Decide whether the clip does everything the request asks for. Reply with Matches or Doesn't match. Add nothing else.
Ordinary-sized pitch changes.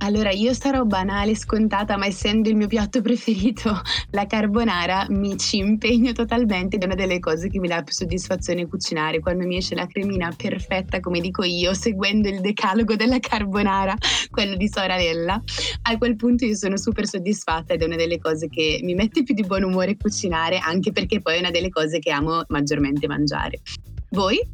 Matches